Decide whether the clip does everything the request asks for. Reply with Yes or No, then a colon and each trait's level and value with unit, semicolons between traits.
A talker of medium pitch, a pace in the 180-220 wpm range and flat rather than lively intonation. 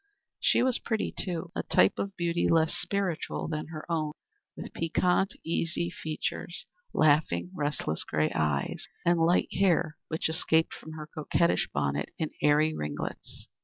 No: medium, 160 Hz; average, 145 wpm; narrow, 2.3 semitones